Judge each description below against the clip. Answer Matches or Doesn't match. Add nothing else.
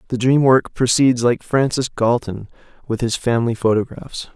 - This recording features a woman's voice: Doesn't match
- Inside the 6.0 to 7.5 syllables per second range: Doesn't match